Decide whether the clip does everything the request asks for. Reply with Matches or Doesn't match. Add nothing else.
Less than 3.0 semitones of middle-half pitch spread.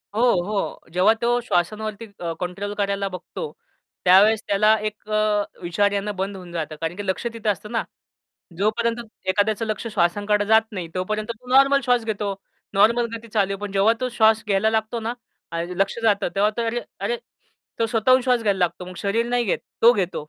Matches